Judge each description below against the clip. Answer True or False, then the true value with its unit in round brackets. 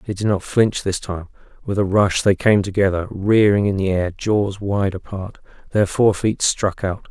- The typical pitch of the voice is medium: False (100 Hz)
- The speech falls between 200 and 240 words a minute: True (205 wpm)